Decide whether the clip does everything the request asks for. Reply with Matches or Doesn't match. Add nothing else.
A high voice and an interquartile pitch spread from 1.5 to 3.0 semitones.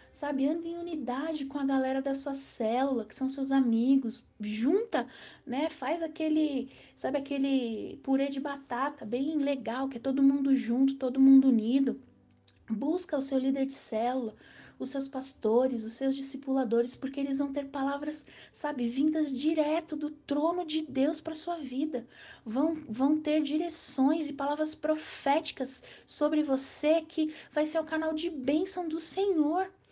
Matches